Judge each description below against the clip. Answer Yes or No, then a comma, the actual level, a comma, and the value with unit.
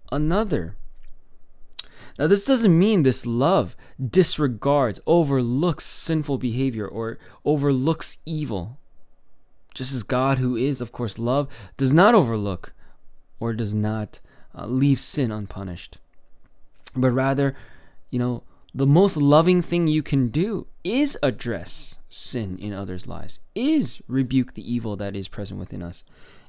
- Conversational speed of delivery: No, slow, 130 wpm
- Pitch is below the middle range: Yes, low, 130 Hz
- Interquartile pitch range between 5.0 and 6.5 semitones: Yes, wide, 5.4 semitones